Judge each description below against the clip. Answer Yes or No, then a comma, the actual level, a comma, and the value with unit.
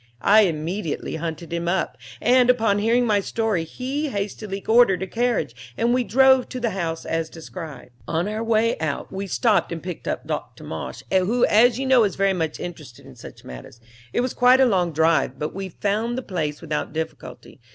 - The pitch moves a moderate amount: No, wide, 6.2 semitones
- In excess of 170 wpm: Yes, average, 195 wpm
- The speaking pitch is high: Yes, high, 195 Hz